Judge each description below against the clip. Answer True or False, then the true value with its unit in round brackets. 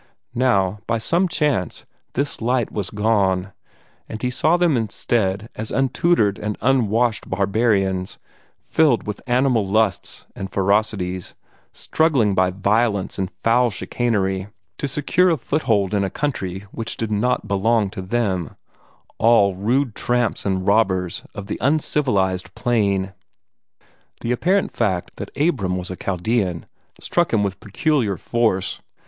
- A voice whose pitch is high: False (110 Hz)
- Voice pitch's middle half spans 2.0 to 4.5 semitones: True (4.2 semitones)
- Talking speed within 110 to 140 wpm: True (135 wpm)